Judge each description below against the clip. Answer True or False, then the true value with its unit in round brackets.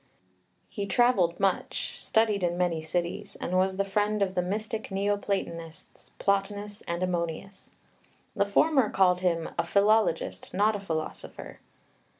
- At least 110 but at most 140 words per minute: True (135 wpm)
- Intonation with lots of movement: False (2.7 semitones)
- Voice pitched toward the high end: True (195 Hz)